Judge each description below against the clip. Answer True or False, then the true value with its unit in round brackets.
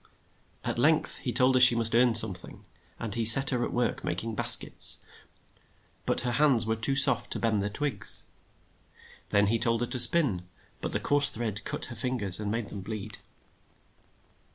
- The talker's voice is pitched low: True (115 Hz)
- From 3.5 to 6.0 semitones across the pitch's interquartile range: False (2.9 semitones)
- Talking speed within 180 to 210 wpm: True (200 wpm)